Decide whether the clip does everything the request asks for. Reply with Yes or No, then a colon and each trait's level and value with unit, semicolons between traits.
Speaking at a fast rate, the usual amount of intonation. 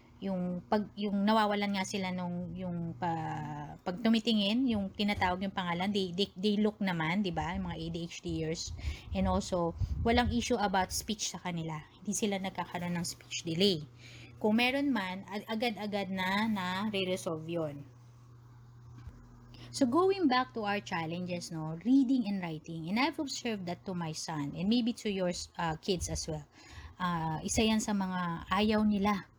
Yes: fast, 165 wpm; average, 4.3 semitones